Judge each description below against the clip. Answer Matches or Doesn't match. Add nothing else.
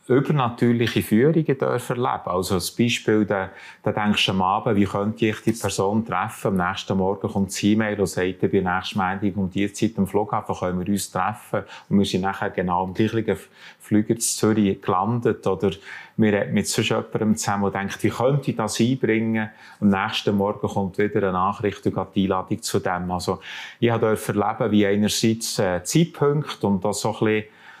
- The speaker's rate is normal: Doesn't match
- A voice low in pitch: Matches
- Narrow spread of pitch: Matches